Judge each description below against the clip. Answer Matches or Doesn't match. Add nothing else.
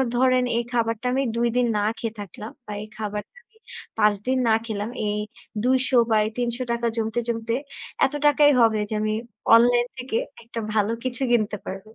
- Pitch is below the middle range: Doesn't match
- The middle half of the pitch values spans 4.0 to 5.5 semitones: Doesn't match